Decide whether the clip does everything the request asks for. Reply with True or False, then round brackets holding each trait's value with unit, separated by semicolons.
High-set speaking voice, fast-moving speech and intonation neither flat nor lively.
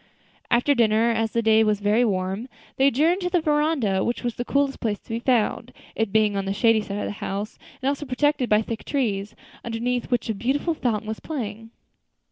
True (230 Hz; 210 wpm; 4.0 semitones)